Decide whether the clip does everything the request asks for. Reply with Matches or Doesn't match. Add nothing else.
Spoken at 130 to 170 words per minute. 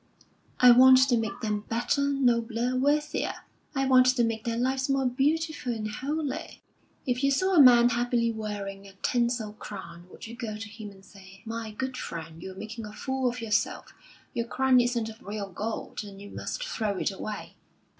Doesn't match